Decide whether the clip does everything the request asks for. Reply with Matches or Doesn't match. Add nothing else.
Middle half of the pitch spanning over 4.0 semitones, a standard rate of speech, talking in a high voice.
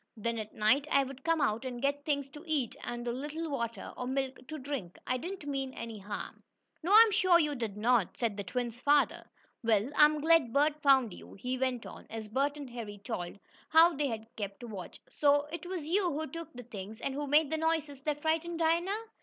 Doesn't match